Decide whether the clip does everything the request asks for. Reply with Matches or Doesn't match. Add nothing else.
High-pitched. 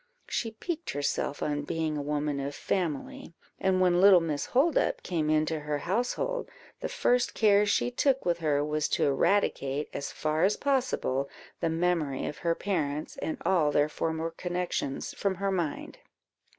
Doesn't match